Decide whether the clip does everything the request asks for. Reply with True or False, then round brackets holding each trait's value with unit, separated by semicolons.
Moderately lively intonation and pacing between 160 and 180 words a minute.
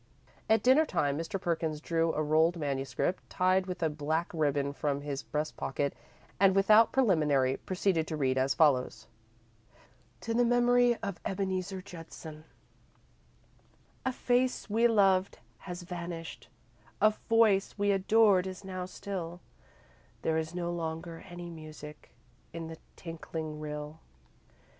False (4.1 semitones; 135 wpm)